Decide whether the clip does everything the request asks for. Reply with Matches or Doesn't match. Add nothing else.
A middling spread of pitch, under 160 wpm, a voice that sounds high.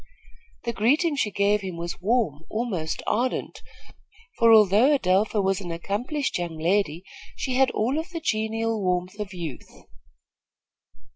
Matches